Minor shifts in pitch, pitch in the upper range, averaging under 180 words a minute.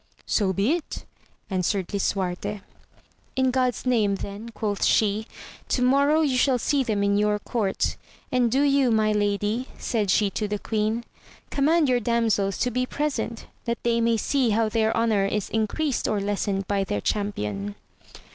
No: average, 3.8 semitones; high, 220 Hz; average, 165 wpm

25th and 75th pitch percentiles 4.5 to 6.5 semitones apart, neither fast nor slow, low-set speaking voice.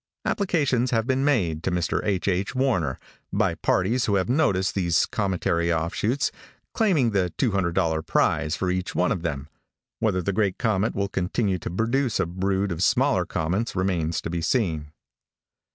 Yes: average, 5.1 semitones; average, 165 wpm; very low, 95 Hz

